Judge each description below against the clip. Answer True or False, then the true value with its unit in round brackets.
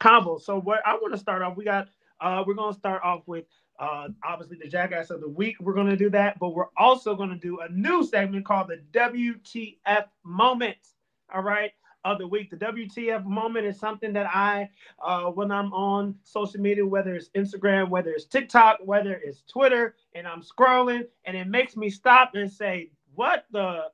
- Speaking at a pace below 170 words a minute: False (205 wpm)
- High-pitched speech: True (200 Hz)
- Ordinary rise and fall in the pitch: True (3.0 semitones)